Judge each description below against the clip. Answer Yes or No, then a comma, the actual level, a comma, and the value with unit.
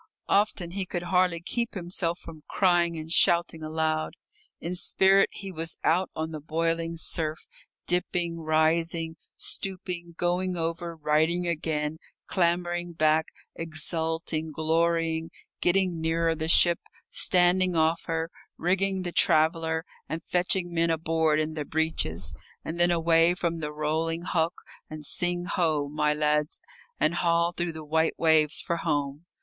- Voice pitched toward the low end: No, medium, 165 Hz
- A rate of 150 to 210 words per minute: No, average, 140 wpm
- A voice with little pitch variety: Yes, narrow, 1.7 semitones